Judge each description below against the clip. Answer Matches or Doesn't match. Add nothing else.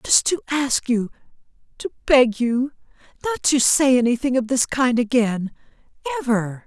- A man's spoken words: Doesn't match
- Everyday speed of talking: Doesn't match